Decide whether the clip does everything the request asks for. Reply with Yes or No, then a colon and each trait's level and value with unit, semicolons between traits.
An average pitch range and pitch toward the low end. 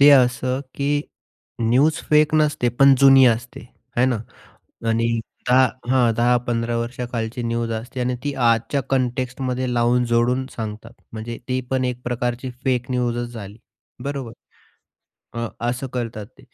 No: narrow, 1.8 semitones; low, 125 Hz